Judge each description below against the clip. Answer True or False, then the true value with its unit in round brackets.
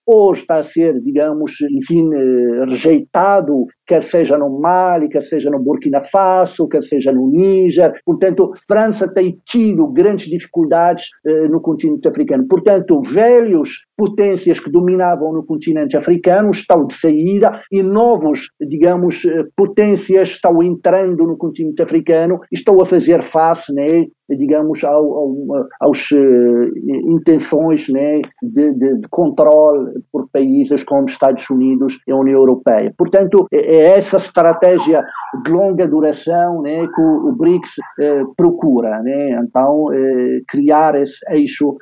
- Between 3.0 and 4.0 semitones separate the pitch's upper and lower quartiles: False (4.6 semitones)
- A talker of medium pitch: True (165 Hz)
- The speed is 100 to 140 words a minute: True (135 wpm)